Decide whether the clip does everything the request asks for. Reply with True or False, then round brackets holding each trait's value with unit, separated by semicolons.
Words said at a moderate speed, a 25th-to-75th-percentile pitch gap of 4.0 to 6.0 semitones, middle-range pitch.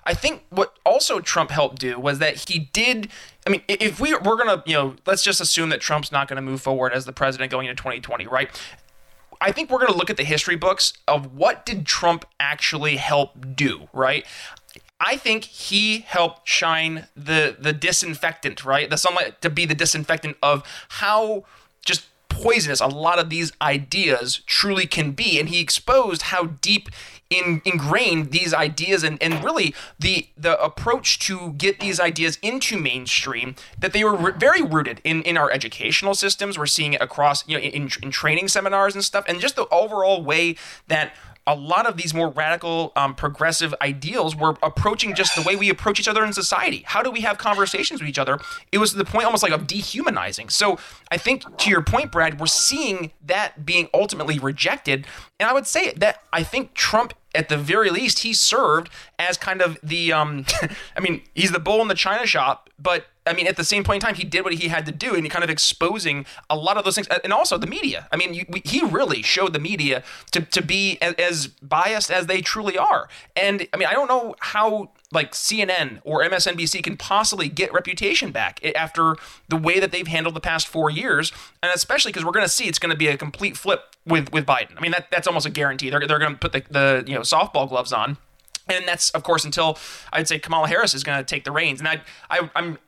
False (220 wpm; 4.3 semitones; 165 Hz)